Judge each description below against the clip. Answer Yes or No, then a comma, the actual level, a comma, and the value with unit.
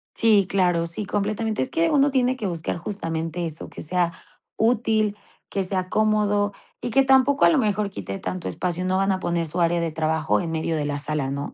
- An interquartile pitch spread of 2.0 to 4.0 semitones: No, average, 4.5 semitones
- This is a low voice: No, high, 190 Hz